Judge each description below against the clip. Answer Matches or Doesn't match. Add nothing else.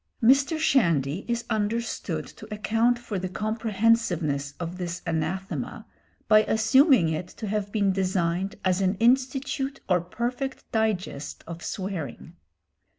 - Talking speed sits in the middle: Doesn't match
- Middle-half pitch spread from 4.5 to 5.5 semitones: Matches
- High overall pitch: Matches